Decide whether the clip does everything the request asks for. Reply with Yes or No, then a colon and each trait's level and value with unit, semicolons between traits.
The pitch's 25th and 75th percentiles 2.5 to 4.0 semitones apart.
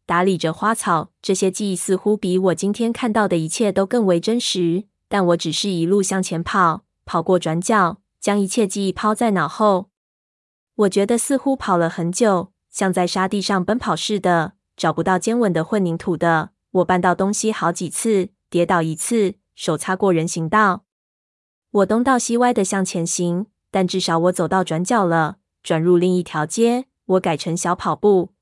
Yes: average, 3.4 semitones